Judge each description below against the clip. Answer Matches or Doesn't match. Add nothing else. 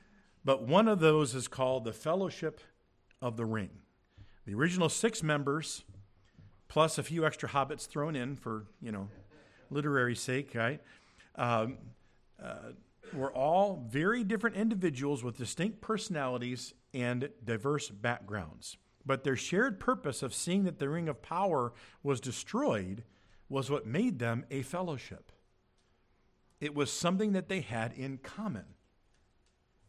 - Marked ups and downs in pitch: Matches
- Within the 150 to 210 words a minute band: Doesn't match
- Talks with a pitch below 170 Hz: Matches